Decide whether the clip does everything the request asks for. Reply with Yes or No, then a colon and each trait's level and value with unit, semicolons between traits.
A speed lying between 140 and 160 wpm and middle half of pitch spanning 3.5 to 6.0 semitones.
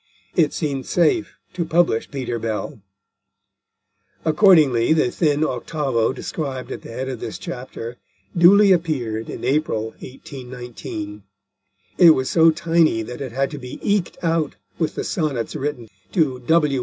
Yes: average, 145 wpm; average, 4.9 semitones